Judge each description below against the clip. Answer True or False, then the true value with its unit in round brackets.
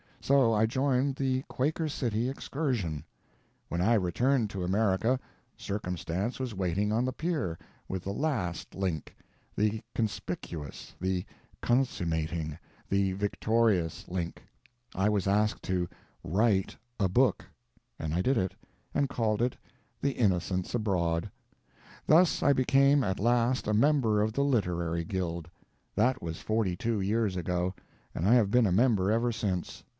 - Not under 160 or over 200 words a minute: False (140 wpm)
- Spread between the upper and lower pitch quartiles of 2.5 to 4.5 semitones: False (5.3 semitones)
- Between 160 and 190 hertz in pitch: False (105 Hz)